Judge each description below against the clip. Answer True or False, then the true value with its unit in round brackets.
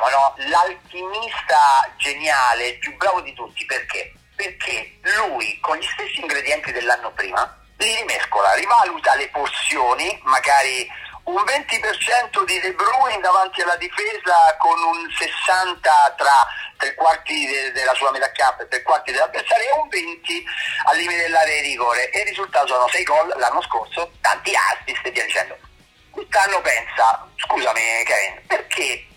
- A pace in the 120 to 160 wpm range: True (145 wpm)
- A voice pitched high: True (205 Hz)